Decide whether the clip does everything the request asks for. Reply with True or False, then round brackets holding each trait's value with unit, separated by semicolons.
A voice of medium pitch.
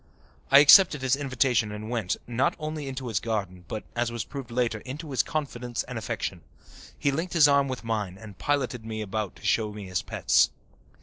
False (120 Hz)